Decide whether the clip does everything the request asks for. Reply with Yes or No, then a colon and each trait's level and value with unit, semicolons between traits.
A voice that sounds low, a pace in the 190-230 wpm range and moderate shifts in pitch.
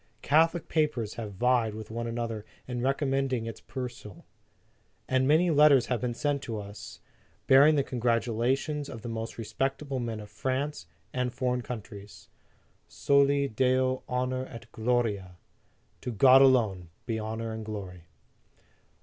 No: low, 125 Hz; average, 140 wpm; average, 3.3 semitones